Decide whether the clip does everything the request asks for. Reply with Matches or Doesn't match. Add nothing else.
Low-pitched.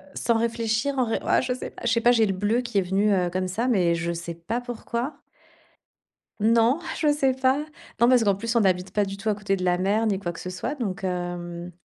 Doesn't match